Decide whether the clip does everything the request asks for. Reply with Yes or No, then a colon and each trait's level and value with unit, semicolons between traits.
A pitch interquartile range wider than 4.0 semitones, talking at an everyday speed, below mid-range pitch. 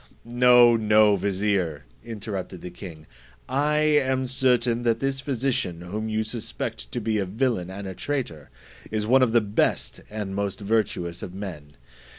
Yes: average, 4.5 semitones; average, 160 wpm; low, 110 Hz